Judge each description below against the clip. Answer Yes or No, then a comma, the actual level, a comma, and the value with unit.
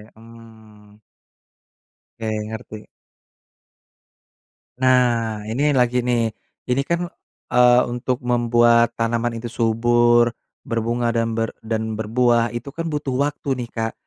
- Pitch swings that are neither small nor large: No, narrow, 1.5 semitones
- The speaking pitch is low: Yes, low, 120 Hz